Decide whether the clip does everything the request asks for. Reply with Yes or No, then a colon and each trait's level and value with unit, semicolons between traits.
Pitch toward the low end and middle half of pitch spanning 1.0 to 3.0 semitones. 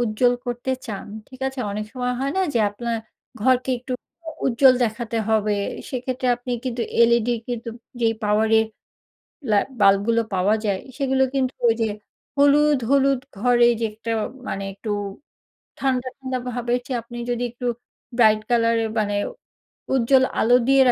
No: high, 240 Hz; average, 2.7 semitones